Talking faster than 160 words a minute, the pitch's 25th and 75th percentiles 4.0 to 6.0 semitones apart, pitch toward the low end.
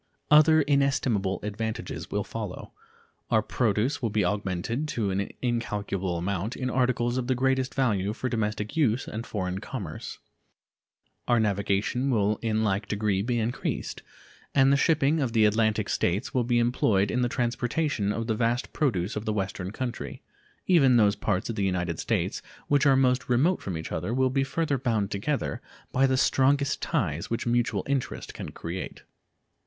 Yes: average, 170 wpm; average, 4.4 semitones; low, 115 Hz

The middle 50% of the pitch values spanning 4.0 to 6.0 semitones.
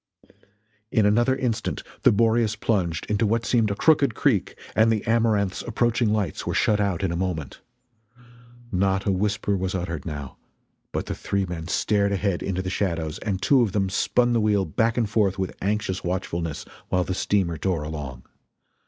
No: average, 3.4 semitones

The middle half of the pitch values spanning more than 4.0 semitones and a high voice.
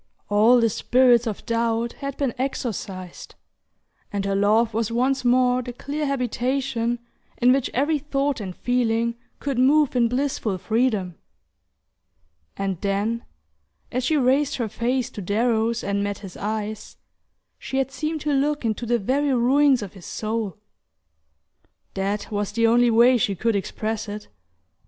No: average, 3.6 semitones; high, 235 Hz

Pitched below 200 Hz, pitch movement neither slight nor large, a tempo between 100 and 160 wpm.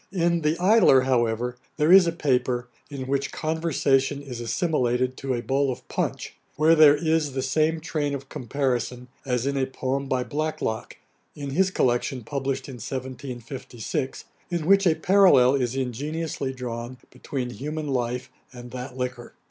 Yes: low, 135 Hz; average, 3.6 semitones; average, 155 wpm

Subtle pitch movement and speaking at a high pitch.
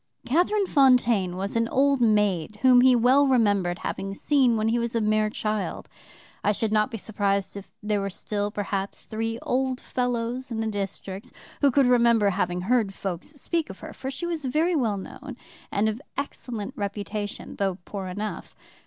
No: average, 3.9 semitones; high, 220 Hz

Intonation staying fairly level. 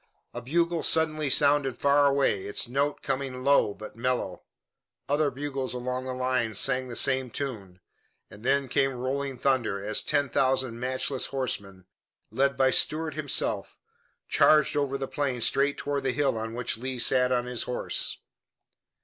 Yes: narrow, 2.2 semitones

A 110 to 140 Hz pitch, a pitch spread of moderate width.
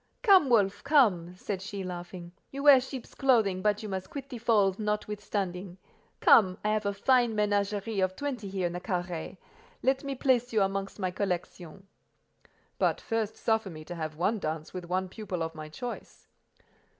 No: high, 200 Hz; average, 3.8 semitones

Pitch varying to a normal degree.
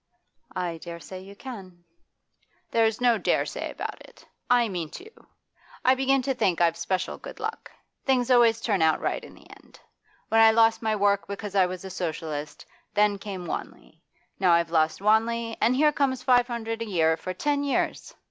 Yes: average, 5.0 semitones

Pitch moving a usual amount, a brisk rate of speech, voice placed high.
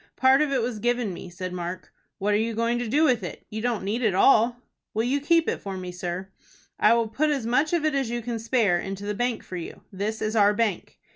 Yes: average, 3.9 semitones; fast, 260 wpm; high, 225 Hz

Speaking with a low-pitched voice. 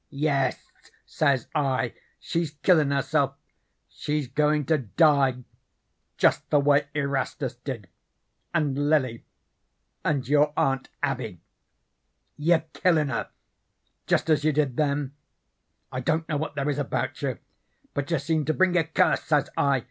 No: medium, 145 Hz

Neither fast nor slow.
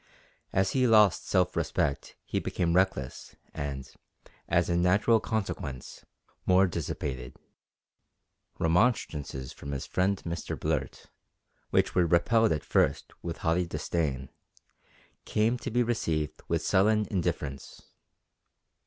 No: slow, 115 wpm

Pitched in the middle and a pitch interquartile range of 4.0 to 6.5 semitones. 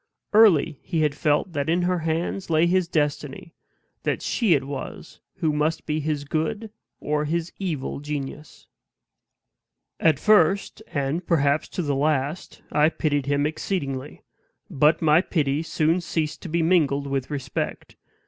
No: medium, 155 Hz; average, 2.9 semitones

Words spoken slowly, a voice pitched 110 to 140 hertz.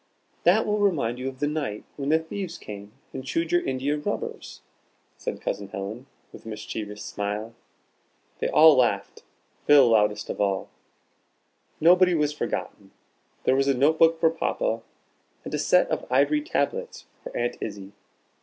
No: average, 155 wpm; low, 135 Hz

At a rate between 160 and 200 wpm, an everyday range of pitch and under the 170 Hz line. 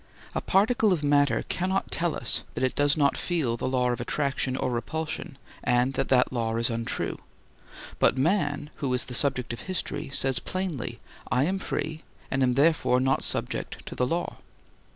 Yes: average, 180 wpm; average, 4.1 semitones; low, 135 Hz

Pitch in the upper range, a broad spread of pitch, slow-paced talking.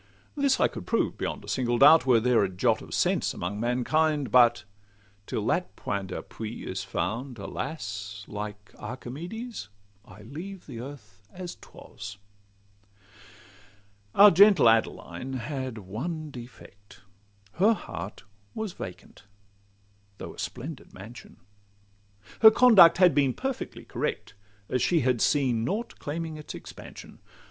No: low, 125 Hz; wide, 7.4 semitones; slow, 130 wpm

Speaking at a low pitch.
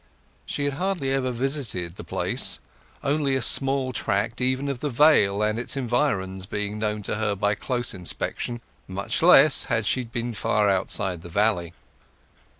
Yes: low, 115 Hz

